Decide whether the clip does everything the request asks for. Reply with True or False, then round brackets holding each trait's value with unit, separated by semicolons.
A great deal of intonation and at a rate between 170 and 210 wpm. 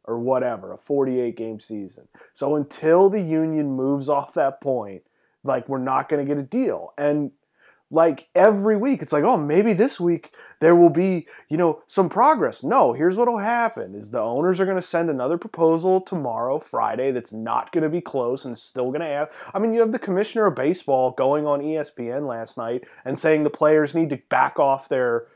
True (5.7 semitones; 200 wpm)